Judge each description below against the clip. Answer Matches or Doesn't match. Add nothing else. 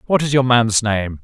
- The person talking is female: Doesn't match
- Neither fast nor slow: Doesn't match